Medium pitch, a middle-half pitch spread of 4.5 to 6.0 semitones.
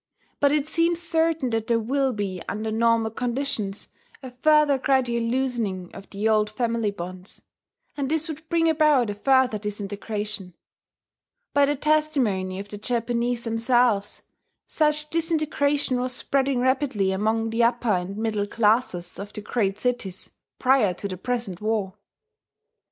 No: high, 235 Hz; average, 4.9 semitones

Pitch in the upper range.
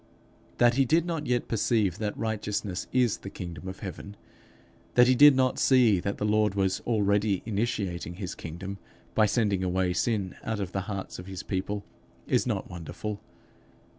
No: low, 105 Hz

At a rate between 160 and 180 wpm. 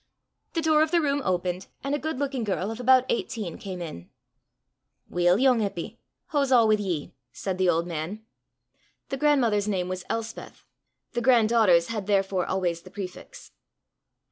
Yes: average, 170 wpm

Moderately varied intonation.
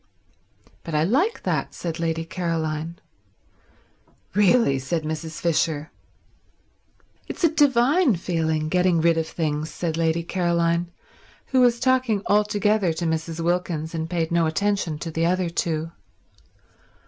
Yes: average, 3.7 semitones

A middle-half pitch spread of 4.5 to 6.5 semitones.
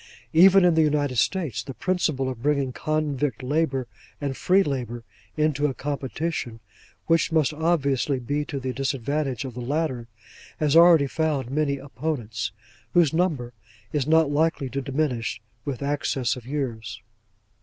No: average, 3.4 semitones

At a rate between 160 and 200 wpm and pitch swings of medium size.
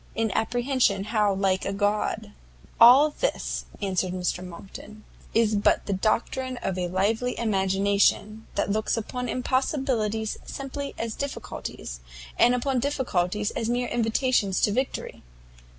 No: slow, 135 wpm; average, 3.9 semitones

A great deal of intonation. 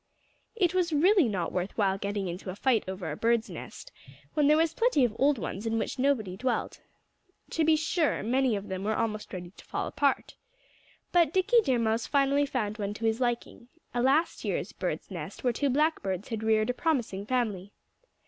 Yes: wide, 5.9 semitones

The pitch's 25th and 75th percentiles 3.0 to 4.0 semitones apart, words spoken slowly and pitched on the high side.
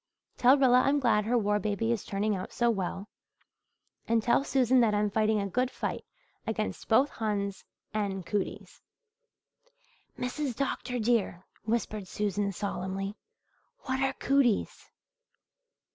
Yes: average, 3.6 semitones; slow, 130 wpm; high, 215 Hz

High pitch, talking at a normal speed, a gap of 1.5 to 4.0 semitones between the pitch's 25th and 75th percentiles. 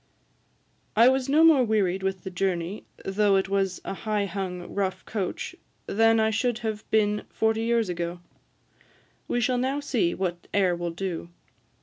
Yes: high, 200 Hz; average, 160 wpm; average, 3.3 semitones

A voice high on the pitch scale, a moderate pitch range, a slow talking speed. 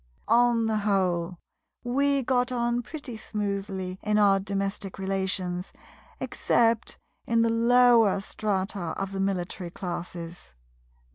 Yes: high, 200 Hz; average, 3.6 semitones; slow, 115 wpm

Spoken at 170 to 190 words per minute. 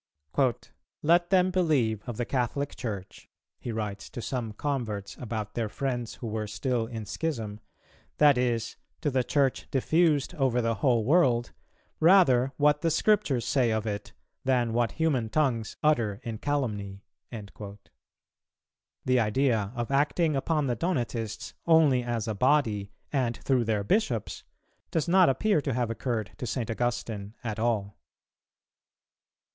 No: average, 140 wpm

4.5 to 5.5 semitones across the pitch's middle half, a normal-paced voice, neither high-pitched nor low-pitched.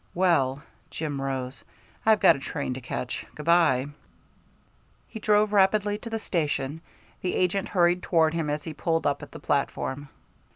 Yes: average, 5.1 semitones; average, 165 wpm; medium, 160 Hz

